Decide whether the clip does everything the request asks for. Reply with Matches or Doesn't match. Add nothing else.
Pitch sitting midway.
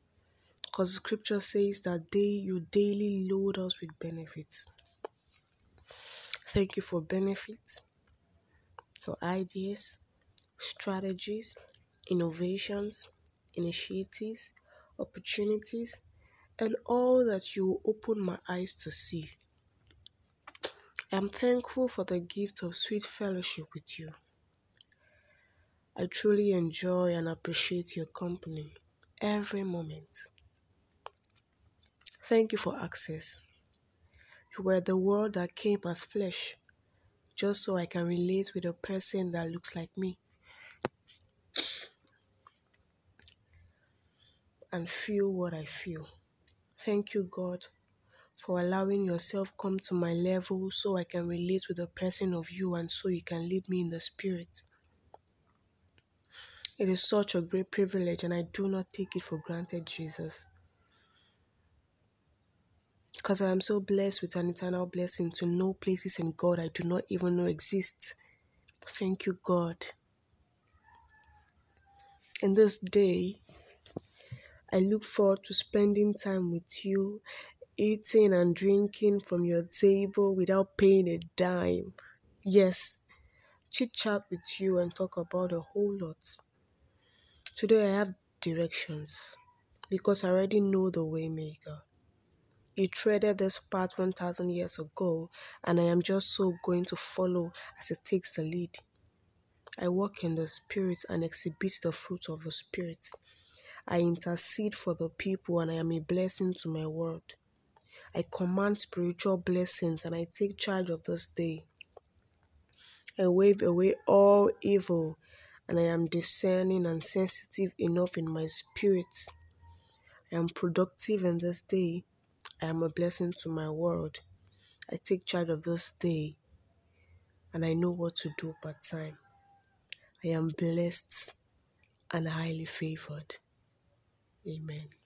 Matches